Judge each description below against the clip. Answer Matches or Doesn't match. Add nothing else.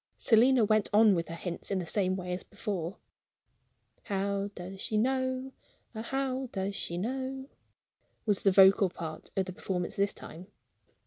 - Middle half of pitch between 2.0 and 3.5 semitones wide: Doesn't match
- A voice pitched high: Matches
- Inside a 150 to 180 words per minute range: Matches